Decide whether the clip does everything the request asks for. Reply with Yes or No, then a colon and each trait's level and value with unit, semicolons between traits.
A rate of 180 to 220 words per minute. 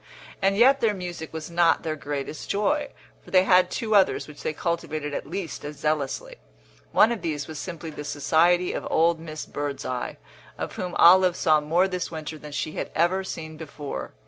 Yes: average, 190 wpm